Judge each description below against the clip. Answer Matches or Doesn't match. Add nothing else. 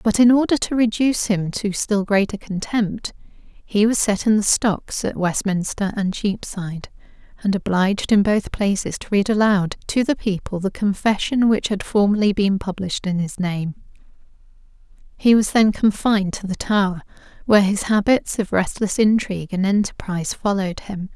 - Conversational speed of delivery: Matches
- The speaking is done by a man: Doesn't match